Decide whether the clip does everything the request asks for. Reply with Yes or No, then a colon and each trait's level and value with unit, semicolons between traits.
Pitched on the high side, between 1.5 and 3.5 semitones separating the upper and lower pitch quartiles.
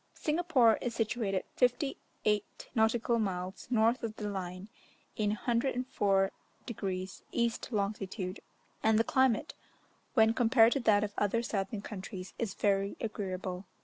Yes: high, 215 Hz; average, 3.2 semitones